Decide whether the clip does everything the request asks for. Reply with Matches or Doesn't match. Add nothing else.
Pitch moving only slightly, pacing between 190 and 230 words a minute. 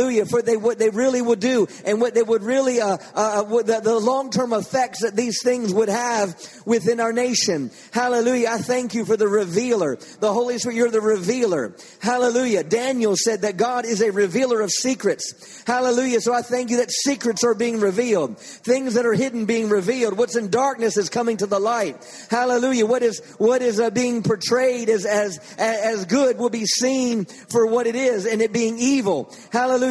Matches